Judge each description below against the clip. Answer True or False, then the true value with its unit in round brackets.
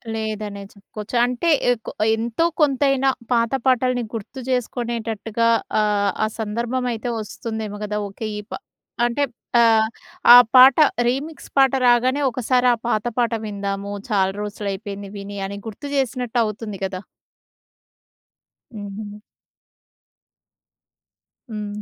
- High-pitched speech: True (225 Hz)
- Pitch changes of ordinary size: True (3.1 semitones)